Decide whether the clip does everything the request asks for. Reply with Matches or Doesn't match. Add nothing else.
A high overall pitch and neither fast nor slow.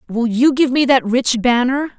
Doesn't match